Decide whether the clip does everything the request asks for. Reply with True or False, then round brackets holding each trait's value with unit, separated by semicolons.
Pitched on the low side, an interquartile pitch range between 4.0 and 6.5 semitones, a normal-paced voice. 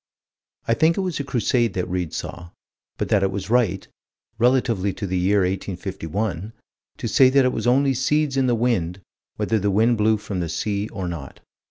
True (105 Hz; 5.0 semitones; 195 wpm)